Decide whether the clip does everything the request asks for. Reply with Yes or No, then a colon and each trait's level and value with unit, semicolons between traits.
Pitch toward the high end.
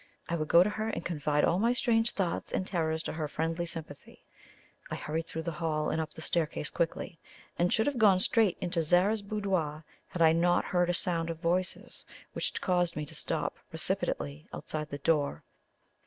No: medium, 170 Hz